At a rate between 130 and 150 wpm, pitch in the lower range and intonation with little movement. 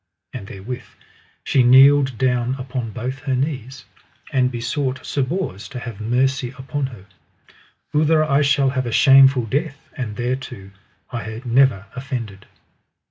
Yes: slow, 135 wpm; low, 130 Hz; narrow, 2.3 semitones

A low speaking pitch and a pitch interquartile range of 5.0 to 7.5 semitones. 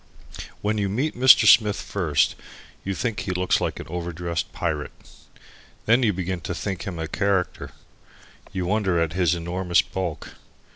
No: very low, 90 Hz; average, 3.0 semitones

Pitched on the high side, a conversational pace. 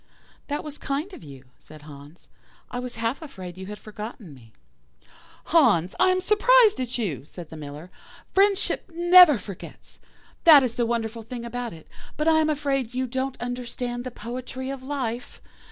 Yes: high, 245 Hz; average, 170 wpm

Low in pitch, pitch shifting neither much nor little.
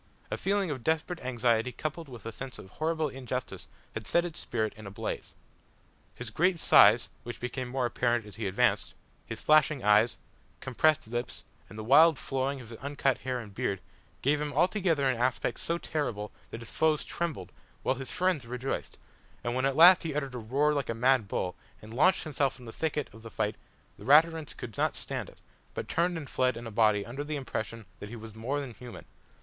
Yes: low, 130 Hz; average, 4.9 semitones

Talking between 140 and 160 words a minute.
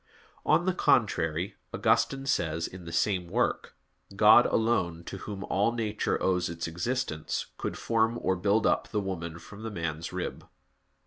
Yes: average, 155 wpm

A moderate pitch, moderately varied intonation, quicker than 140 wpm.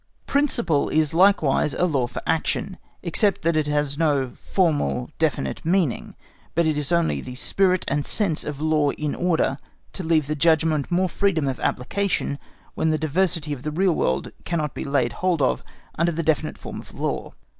Yes: medium, 155 Hz; average, 3.3 semitones; average, 190 wpm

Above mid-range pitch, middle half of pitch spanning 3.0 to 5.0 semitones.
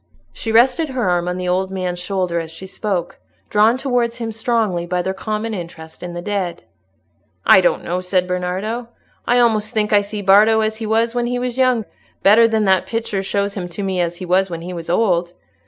Yes: high, 200 Hz; average, 3.9 semitones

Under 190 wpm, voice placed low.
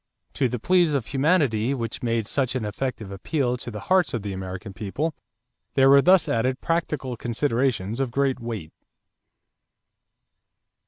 Yes: average, 150 wpm; low, 125 Hz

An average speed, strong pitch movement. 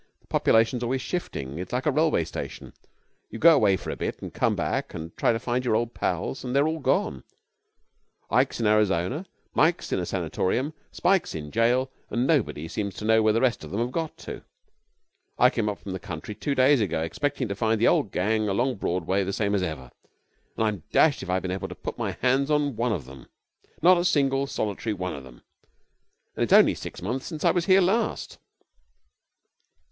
No: fast, 210 wpm; wide, 6.5 semitones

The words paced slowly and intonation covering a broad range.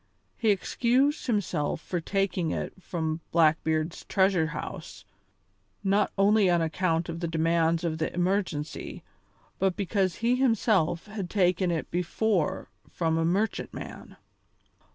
No: slow, 125 wpm; average, 3.5 semitones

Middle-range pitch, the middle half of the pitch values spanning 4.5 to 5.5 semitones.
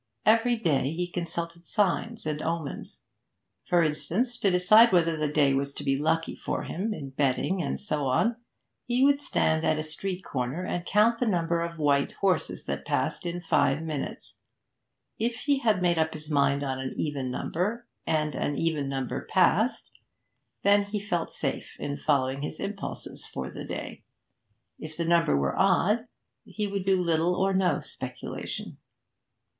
Yes: medium, 170 Hz; average, 5.0 semitones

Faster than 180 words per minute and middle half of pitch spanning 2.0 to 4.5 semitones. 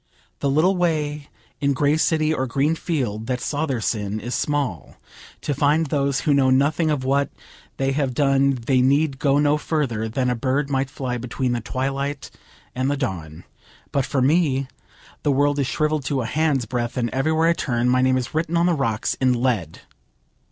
Yes: average, 190 wpm; average, 2.7 semitones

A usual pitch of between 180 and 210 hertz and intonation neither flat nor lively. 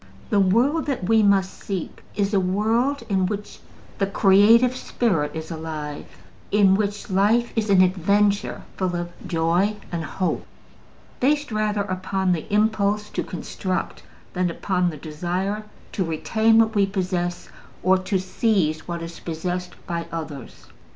Yes: high, 190 Hz; average, 3.1 semitones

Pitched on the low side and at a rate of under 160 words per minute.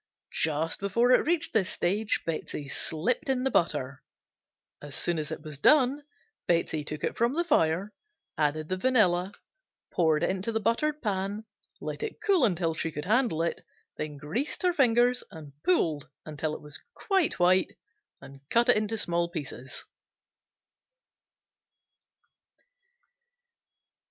No: medium, 185 Hz; slow, 135 wpm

